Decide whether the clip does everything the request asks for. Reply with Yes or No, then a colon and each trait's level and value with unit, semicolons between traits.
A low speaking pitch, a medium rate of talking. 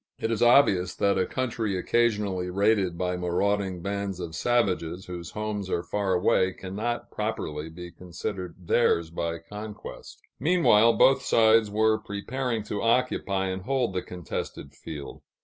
Yes: low, 100 Hz; average, 145 wpm